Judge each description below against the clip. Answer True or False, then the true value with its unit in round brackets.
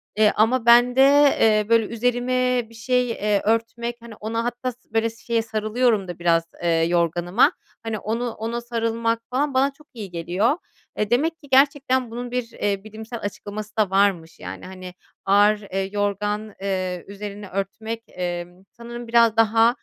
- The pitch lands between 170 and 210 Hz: False (225 Hz)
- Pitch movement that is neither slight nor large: True (3.1 semitones)